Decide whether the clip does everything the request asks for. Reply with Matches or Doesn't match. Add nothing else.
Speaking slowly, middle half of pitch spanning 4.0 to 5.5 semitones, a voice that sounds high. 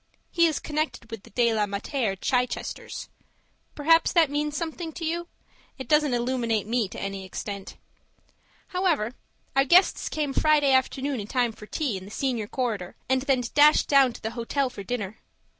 Doesn't match